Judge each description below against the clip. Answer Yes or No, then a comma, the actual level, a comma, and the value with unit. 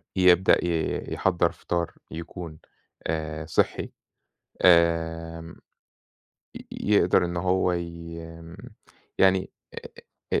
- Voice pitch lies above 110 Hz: No, very low, 85 Hz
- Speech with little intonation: Yes, narrow, 1.2 semitones